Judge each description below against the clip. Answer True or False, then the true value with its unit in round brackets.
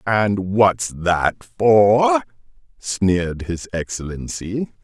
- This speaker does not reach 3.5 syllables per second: True (2.9 syllables/s)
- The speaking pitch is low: True (105 Hz)